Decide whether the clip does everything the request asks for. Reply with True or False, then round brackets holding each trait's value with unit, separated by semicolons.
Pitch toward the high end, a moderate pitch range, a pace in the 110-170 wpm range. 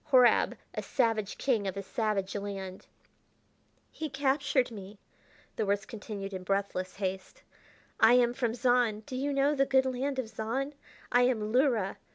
True (230 Hz; 4.7 semitones; 160 wpm)